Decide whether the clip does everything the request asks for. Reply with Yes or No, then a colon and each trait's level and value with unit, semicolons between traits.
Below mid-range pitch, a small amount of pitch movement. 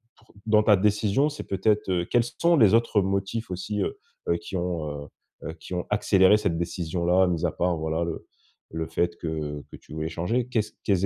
No: very low, 95 Hz; average, 4.0 semitones